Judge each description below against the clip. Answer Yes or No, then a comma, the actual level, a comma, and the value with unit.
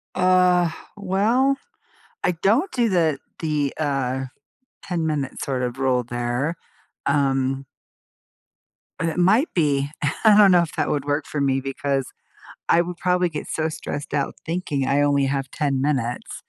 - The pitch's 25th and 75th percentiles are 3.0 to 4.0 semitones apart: No, average, 4.7 semitones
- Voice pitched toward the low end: No, medium, 150 Hz